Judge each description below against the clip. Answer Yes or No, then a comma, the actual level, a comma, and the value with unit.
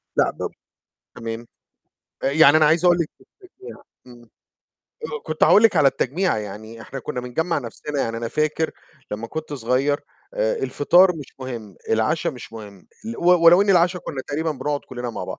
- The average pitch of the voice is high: No, medium, 145 Hz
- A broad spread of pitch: Yes, wide, 6.3 semitones